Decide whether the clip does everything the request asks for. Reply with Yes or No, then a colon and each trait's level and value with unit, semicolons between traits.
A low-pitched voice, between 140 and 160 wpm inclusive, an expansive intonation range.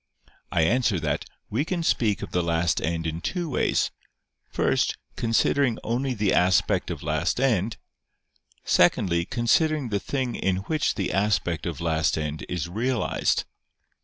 Yes: low, 100 Hz; average, 145 wpm; wide, 6.9 semitones